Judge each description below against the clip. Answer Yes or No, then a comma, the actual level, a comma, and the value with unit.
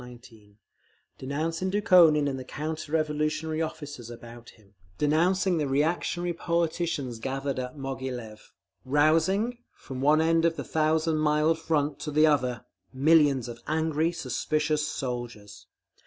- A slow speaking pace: Yes, slow, 125 wpm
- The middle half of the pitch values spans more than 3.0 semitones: Yes, average, 3.6 semitones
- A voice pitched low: No, medium, 150 Hz